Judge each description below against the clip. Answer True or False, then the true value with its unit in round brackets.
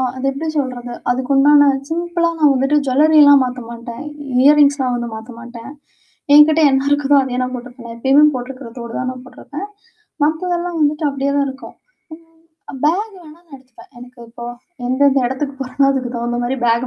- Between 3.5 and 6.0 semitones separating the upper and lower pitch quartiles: False (3.0 semitones)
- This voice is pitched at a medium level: False (270 Hz)